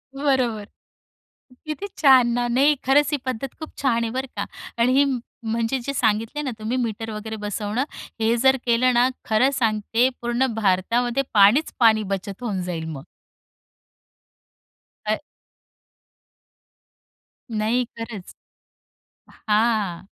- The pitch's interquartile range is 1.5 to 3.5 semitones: Yes, average, 3.2 semitones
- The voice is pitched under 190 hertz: No, high, 235 Hz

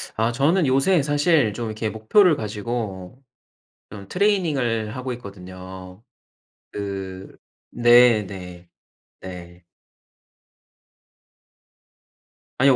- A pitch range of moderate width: No, wide, 6.1 semitones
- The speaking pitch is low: Yes, low, 110 Hz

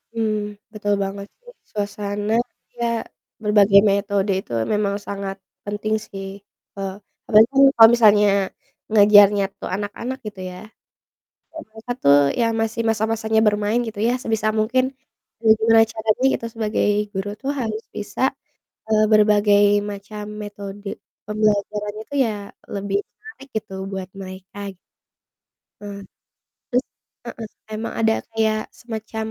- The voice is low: No, high, 210 Hz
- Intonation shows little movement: Yes, narrow, 1.6 semitones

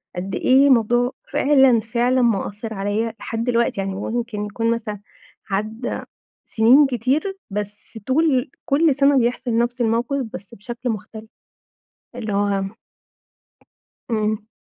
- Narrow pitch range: No, average, 3.2 semitones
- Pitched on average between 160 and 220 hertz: No, high, 230 Hz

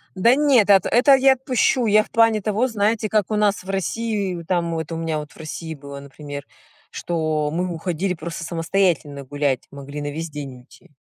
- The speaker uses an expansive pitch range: Yes, wide, 5.9 semitones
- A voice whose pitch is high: No, medium, 175 Hz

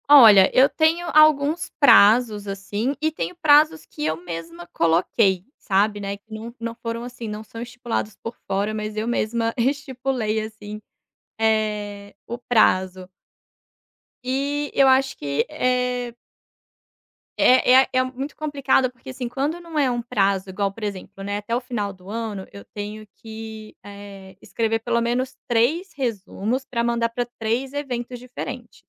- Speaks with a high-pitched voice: Yes, high, 230 Hz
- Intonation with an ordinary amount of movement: Yes, average, 4.0 semitones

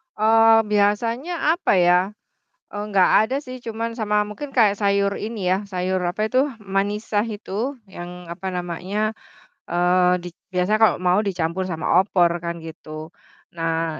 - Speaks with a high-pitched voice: Yes, high, 200 Hz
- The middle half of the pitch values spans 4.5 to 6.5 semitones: No, average, 3.5 semitones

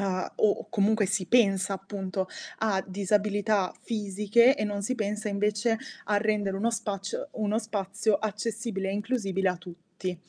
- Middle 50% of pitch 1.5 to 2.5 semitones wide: Yes, narrow, 1.9 semitones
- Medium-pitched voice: No, high, 205 Hz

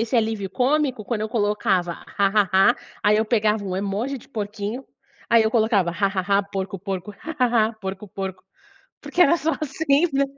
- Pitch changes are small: No, average, 4.1 semitones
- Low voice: No, high, 210 Hz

